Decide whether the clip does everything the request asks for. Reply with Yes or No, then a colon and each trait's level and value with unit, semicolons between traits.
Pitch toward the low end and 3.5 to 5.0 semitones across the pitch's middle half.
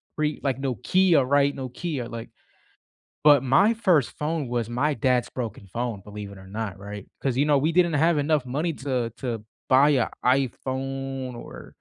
Yes: low, 130 Hz; average, 3.8 semitones